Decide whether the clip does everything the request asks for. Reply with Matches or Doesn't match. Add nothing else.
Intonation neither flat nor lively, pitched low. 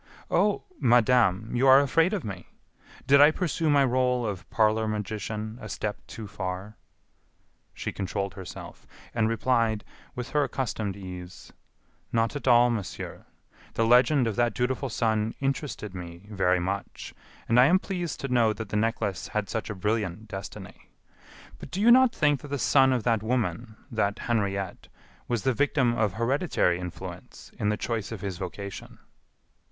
Matches